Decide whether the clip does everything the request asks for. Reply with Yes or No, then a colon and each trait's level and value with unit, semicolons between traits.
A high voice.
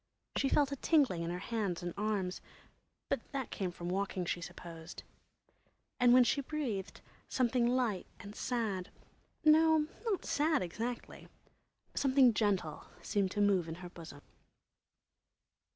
Yes: high, 210 Hz